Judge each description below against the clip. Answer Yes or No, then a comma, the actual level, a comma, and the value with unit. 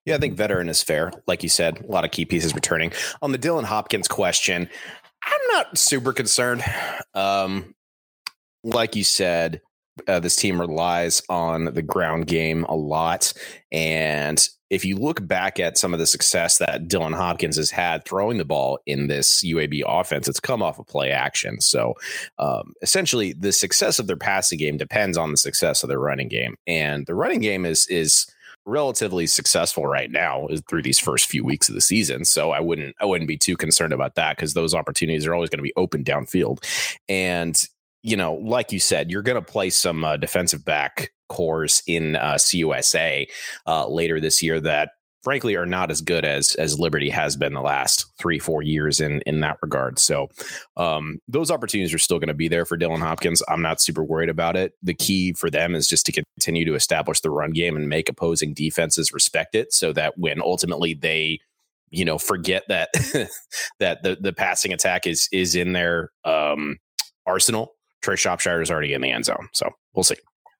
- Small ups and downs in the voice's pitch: Yes, narrow, 2.2 semitones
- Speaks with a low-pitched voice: Yes, very low, 80 Hz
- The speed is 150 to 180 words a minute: No, average, 200 wpm